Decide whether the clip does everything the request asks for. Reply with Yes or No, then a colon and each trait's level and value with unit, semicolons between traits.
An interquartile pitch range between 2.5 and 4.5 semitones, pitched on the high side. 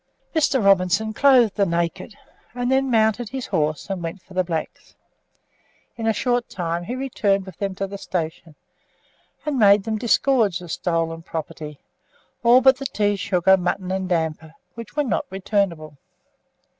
No: average, 5.3 semitones; high, 195 Hz